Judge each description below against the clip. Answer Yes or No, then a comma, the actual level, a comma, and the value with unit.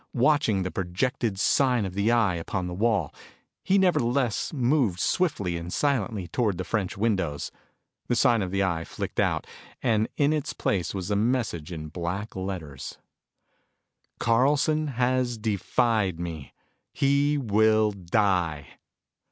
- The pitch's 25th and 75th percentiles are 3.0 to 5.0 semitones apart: No, wide, 5.6 semitones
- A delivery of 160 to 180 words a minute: No, slow, 135 wpm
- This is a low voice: Yes, low, 105 Hz